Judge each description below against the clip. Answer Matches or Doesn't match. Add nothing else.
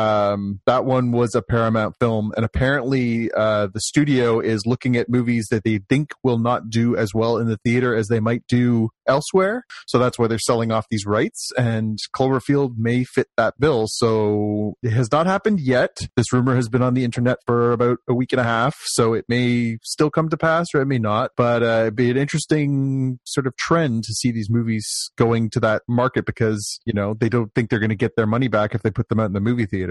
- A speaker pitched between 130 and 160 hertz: Doesn't match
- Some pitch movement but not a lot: Doesn't match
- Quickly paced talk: Matches